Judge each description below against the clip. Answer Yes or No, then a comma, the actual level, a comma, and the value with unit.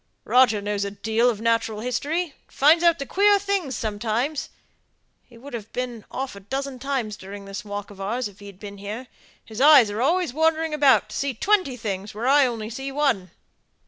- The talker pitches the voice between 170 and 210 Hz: No, high, 245 Hz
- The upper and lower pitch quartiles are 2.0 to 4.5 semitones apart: No, average, 5.1 semitones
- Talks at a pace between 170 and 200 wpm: Yes, average, 190 wpm